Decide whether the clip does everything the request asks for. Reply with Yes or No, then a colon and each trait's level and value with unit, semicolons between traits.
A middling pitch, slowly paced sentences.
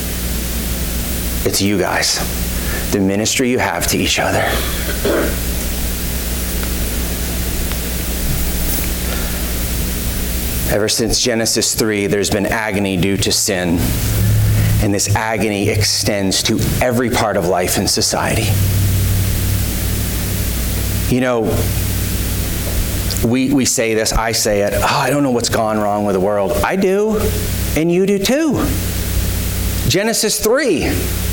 No: very low, 95 Hz; slow, 110 wpm